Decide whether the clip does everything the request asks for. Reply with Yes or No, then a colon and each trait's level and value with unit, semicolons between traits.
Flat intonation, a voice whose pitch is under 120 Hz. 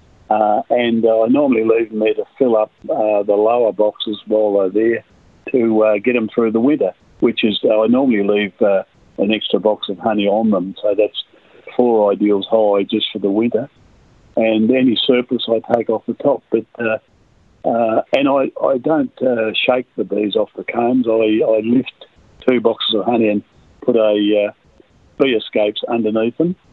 Yes: narrow, 1.9 semitones; low, 110 Hz